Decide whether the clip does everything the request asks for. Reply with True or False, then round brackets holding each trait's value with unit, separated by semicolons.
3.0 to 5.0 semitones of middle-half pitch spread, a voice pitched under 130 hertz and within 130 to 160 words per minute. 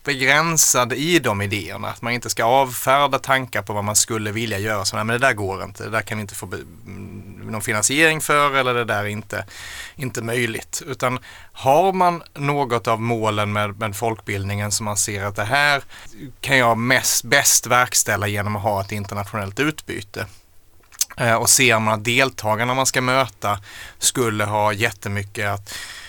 False (3.8 semitones; 110 Hz; 175 wpm)